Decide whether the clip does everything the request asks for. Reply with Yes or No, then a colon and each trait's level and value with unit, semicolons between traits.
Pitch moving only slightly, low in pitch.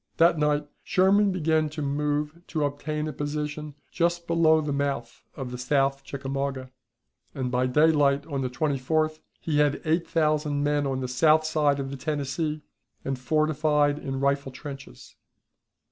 No: narrow, 2.2 semitones; medium, 145 Hz